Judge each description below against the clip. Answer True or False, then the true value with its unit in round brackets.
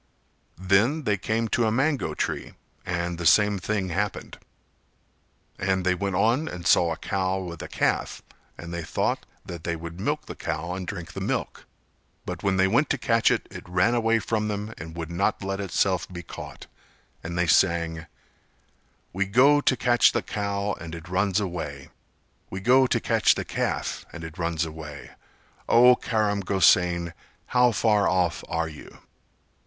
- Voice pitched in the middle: False (95 Hz)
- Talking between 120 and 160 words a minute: False (175 wpm)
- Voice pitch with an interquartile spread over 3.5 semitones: True (4.0 semitones)